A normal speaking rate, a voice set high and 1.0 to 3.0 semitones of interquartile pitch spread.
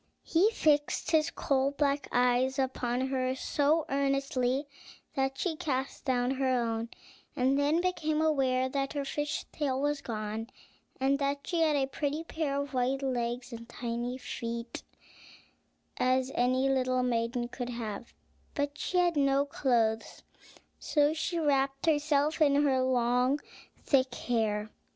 Yes: average, 145 wpm; very high, 270 Hz; average, 2.7 semitones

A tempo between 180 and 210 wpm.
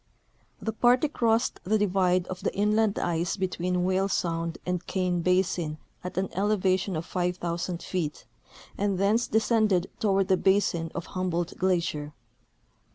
No: average, 145 wpm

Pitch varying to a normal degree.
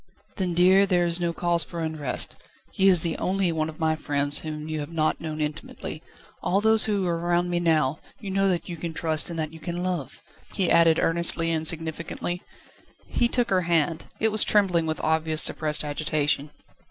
No: narrow, 2.3 semitones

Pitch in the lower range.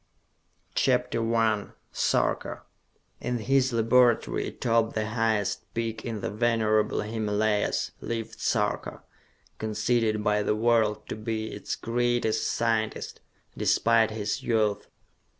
Yes: low, 110 Hz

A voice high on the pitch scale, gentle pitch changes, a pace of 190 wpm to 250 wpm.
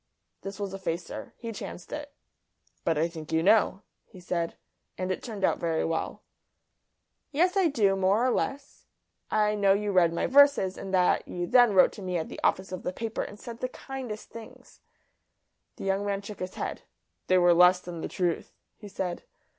No: high, 195 Hz; average, 3.8 semitones; average, 195 wpm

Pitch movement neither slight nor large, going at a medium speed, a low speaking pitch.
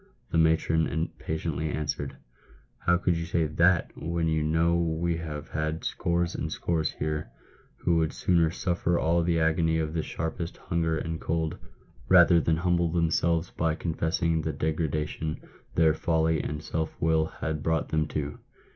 No: narrow, 1.2 semitones; average, 160 wpm; very low, 80 Hz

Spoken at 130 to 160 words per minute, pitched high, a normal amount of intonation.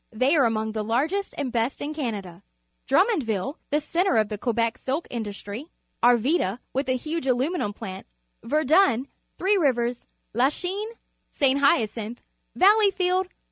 No: average, 140 wpm; very high, 260 Hz; wide, 6.6 semitones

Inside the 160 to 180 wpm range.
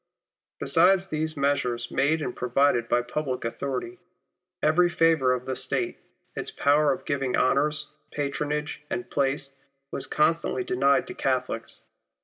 No: slow, 135 wpm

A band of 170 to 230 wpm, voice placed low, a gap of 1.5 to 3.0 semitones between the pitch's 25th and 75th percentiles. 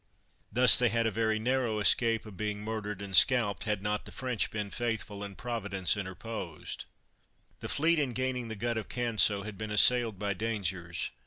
Yes: average, 180 wpm; low, 110 Hz; average, 2.7 semitones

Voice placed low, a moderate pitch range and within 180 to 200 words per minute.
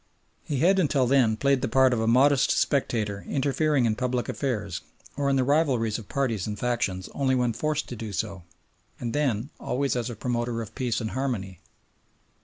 Yes: low, 125 Hz; average, 3.7 semitones; average, 190 wpm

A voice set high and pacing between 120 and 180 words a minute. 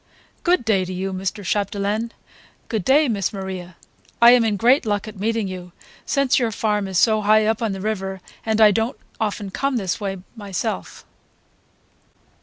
Yes: high, 210 Hz; average, 170 wpm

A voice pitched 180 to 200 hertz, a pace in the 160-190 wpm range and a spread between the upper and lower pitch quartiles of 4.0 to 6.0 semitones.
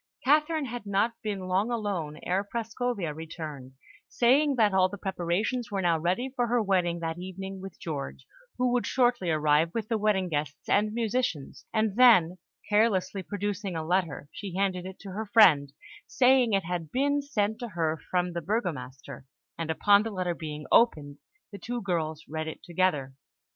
Yes: high, 190 Hz; average, 175 wpm; average, 5.2 semitones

